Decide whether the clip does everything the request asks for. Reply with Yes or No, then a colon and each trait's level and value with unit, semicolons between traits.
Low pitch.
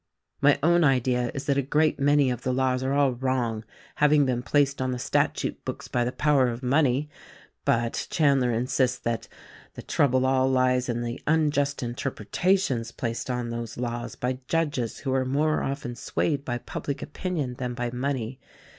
Yes: low, 130 Hz